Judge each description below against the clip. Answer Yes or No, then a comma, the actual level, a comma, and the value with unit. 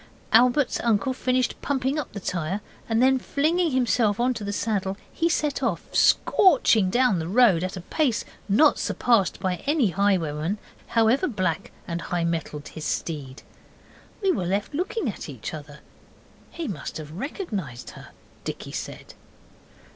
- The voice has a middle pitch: No, high, 210 Hz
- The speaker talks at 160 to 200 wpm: No, average, 150 wpm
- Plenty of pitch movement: Yes, wide, 6.8 semitones